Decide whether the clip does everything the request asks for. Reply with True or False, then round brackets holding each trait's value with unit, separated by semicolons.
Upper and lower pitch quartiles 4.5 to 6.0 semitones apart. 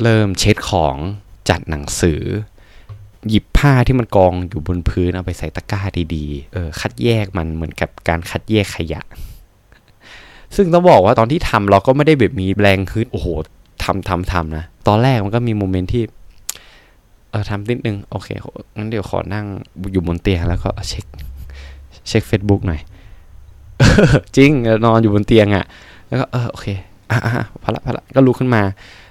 False (3.9 semitones)